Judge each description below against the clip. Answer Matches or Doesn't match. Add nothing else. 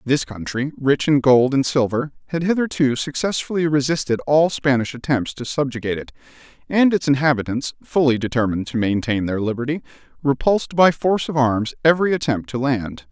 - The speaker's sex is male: Matches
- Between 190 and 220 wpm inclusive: Doesn't match